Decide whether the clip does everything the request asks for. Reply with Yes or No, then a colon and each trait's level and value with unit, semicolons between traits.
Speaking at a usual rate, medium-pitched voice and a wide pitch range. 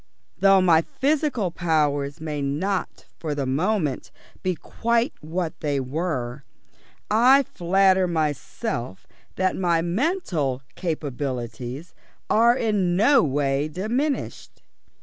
No: slow, 105 wpm; medium, 170 Hz; wide, 6.3 semitones